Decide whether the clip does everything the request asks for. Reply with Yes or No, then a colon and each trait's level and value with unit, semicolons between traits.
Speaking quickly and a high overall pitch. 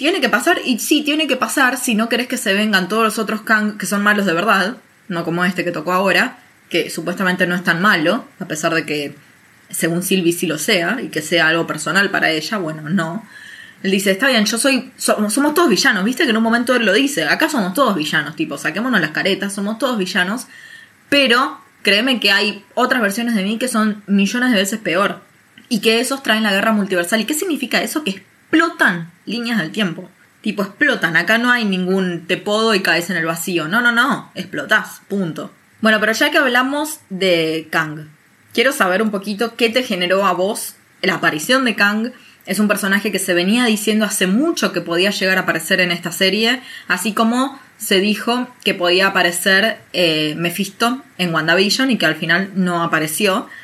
Yes: fast, 205 wpm; high, 205 Hz